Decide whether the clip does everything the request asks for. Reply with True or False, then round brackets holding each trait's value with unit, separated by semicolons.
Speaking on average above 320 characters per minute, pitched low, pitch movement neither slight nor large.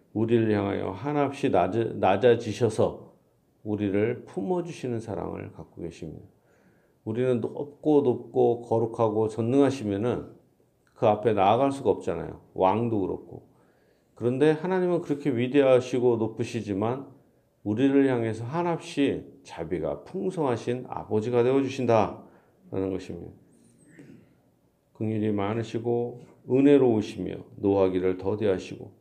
False (285 characters per minute; 120 Hz; 4.1 semitones)